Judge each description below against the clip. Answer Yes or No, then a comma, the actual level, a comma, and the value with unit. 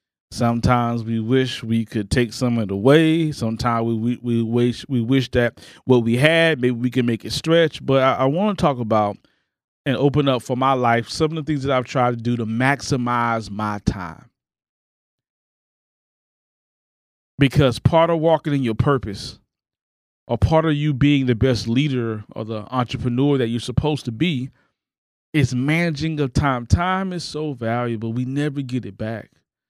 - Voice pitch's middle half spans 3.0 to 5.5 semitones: Yes, average, 3.5 semitones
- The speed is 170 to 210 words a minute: Yes, average, 180 wpm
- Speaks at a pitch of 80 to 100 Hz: No, low, 125 Hz